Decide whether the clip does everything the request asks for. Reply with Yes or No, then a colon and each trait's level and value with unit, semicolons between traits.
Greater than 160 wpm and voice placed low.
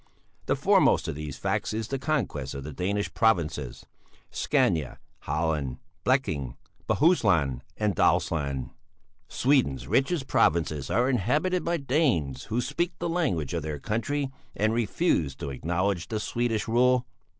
No: average, 140 wpm; low, 100 Hz